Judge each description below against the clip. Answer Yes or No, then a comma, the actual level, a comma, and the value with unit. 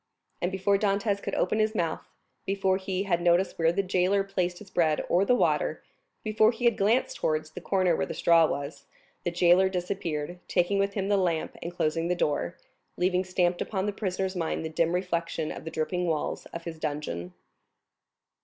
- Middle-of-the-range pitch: Yes, medium, 180 Hz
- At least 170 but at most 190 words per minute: Yes, average, 185 wpm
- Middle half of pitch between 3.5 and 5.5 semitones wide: No, average, 2.9 semitones